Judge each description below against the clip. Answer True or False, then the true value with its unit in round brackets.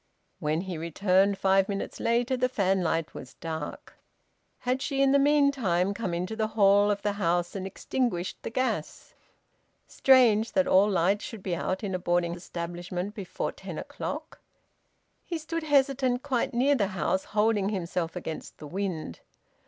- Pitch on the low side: False (200 Hz)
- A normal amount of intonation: False (5.7 semitones)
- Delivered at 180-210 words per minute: False (160 wpm)